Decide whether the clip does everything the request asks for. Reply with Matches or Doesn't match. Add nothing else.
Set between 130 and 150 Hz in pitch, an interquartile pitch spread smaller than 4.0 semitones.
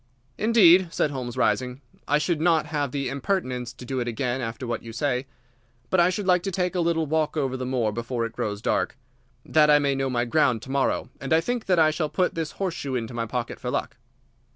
Doesn't match